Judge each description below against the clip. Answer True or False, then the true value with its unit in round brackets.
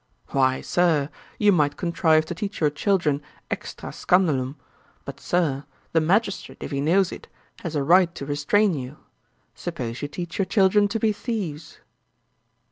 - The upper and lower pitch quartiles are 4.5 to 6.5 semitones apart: True (4.8 semitones)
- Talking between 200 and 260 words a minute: False (155 wpm)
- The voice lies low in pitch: False (165 Hz)